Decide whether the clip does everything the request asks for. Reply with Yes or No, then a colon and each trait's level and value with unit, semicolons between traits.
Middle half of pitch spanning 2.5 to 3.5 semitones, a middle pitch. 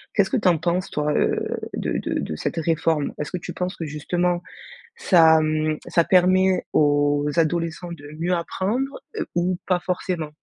Yes: average, 2.9 semitones; medium, 170 Hz